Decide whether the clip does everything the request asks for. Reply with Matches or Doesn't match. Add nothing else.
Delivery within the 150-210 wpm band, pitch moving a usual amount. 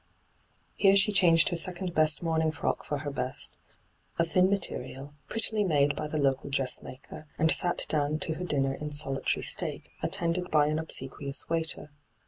Matches